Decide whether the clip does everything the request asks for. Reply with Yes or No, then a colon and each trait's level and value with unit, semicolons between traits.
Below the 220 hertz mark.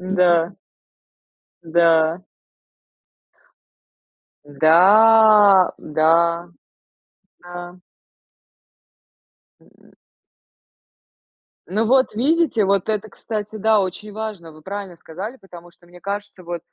Yes: high, 190 Hz